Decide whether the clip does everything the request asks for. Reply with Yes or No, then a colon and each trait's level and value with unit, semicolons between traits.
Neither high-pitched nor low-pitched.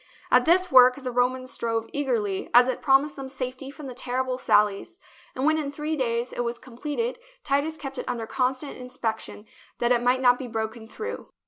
No: very high, 255 Hz